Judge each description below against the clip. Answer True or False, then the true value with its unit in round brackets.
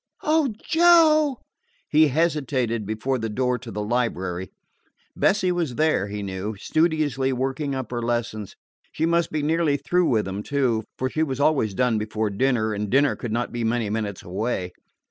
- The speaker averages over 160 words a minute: True (170 wpm)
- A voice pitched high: False (125 Hz)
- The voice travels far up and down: True (6.2 semitones)